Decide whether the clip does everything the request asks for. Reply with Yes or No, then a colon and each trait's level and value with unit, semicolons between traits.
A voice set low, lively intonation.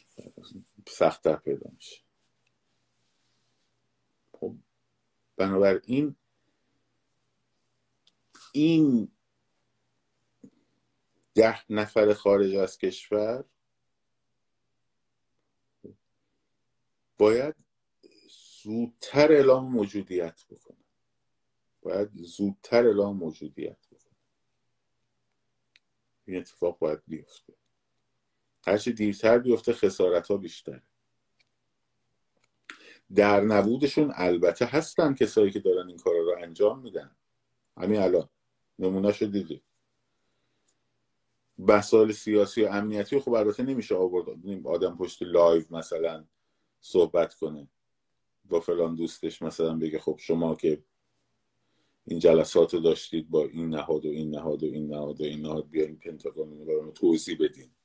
Yes: low, 105 Hz; wide, 7.7 semitones